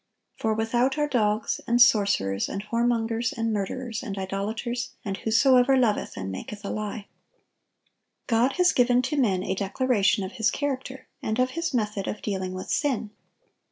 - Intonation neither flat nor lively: Yes, average, 3.8 semitones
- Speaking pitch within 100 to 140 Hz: No, high, 225 Hz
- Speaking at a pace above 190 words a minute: No, average, 160 wpm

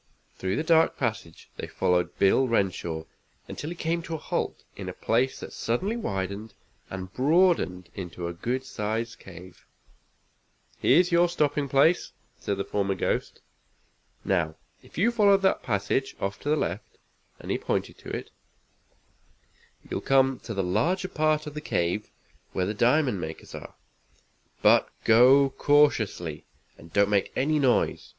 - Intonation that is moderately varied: No, wide, 8.0 semitones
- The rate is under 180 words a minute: Yes, average, 155 wpm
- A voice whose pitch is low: Yes, low, 120 Hz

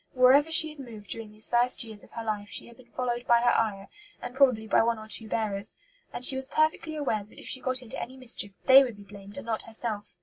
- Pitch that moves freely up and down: No, average, 3.3 semitones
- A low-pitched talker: No, high, 235 Hz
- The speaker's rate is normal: No, fast, 260 wpm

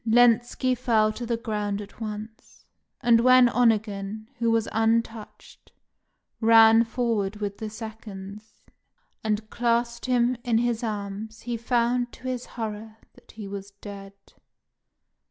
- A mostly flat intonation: Yes, narrow, 2.0 semitones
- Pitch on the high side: Yes, high, 225 Hz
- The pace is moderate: No, slow, 130 wpm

